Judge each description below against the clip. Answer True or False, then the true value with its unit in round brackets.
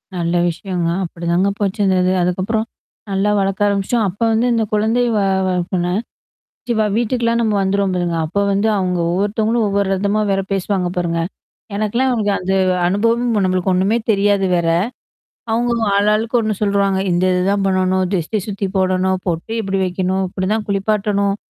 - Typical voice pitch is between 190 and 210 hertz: True (195 Hz)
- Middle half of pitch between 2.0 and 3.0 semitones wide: True (2.4 semitones)